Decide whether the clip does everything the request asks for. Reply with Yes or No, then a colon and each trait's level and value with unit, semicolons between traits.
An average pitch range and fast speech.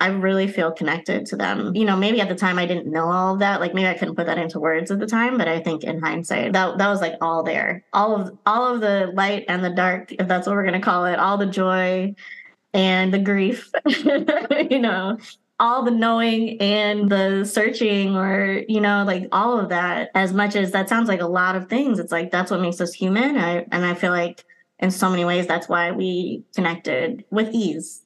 Yes: average, 3.0 semitones; fast, 235 wpm